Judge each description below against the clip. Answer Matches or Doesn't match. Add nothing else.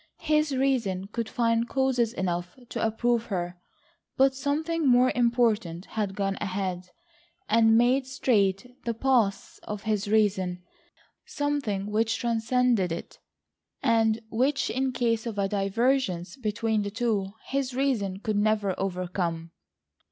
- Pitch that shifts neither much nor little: Matches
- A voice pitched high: Matches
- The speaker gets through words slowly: Matches